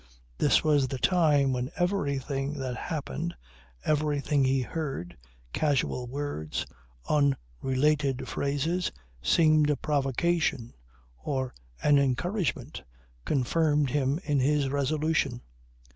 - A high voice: No, medium, 145 Hz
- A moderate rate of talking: No, slow, 100 wpm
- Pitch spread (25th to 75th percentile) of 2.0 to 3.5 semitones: Yes, narrow, 2.5 semitones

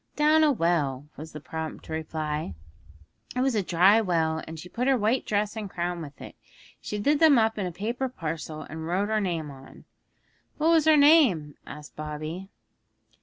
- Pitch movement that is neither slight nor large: No, wide, 6.7 semitones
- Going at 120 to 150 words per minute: No, average, 185 wpm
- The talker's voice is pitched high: No, medium, 180 Hz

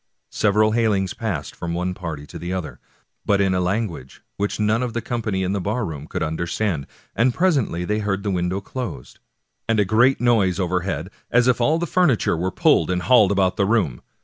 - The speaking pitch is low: Yes, low, 100 Hz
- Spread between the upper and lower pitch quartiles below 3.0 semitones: No, average, 4.1 semitones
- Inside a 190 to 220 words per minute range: Yes, average, 200 wpm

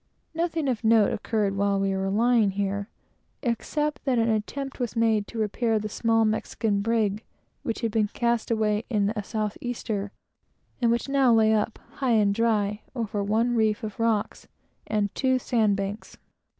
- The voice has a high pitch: Yes, high, 220 Hz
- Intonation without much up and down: Yes, narrow, 2.3 semitones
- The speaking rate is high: No, average, 170 wpm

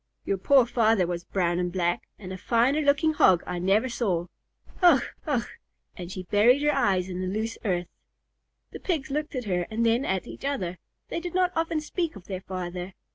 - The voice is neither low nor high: No, high, 210 Hz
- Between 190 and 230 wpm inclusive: Yes, average, 200 wpm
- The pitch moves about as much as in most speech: No, wide, 7.4 semitones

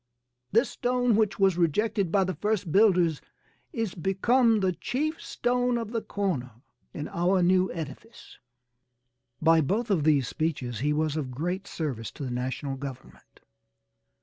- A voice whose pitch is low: No, medium, 180 Hz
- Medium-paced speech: Yes, average, 150 wpm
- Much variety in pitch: Yes, wide, 6.7 semitones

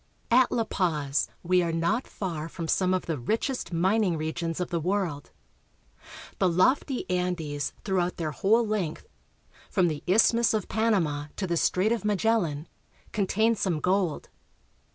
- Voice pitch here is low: No, medium, 180 Hz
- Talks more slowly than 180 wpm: Yes, average, 160 wpm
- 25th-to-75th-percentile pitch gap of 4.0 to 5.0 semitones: Yes, average, 4.5 semitones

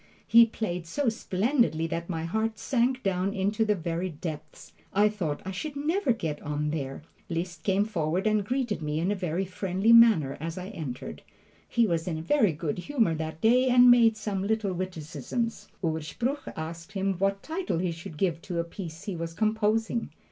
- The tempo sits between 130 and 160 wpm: No, average, 185 wpm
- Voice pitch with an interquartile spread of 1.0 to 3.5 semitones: No, average, 5.2 semitones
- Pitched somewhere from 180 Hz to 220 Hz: Yes, high, 190 Hz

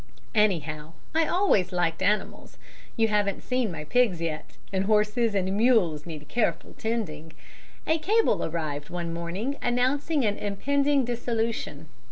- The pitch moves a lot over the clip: Yes, wide, 6.5 semitones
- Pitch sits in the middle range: No, high, 210 Hz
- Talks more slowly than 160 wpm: Yes, slow, 135 wpm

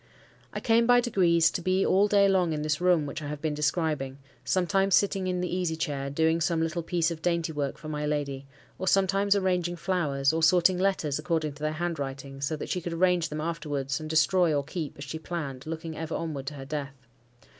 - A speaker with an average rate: No, fast, 220 wpm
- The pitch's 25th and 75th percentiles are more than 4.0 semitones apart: No, average, 3.3 semitones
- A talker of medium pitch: Yes, medium, 160 Hz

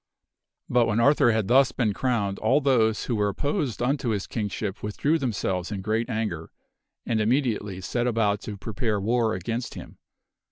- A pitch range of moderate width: Yes, average, 3.1 semitones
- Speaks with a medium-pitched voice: No, low, 110 Hz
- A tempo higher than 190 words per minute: No, average, 165 wpm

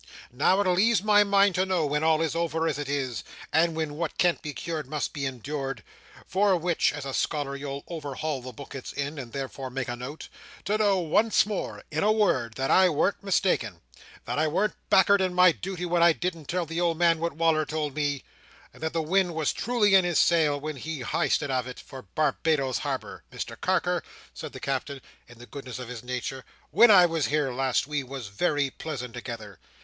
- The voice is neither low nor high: Yes, medium, 155 Hz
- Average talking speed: No, fast, 210 wpm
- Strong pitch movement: No, average, 4.5 semitones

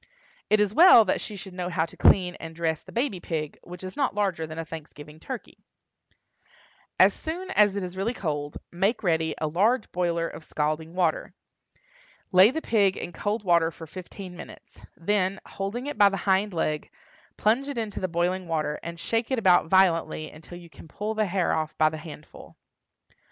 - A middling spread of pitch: Yes, average, 4.2 semitones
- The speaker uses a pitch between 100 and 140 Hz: No, medium, 185 Hz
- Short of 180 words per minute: No, average, 195 wpm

